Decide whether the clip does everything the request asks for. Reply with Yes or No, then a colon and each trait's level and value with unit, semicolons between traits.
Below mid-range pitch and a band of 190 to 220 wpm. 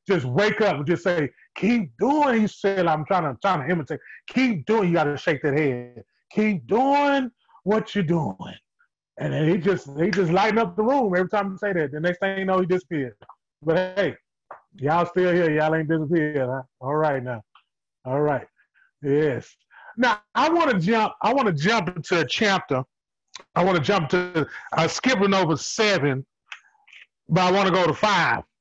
No: medium, 180 Hz; average, 195 wpm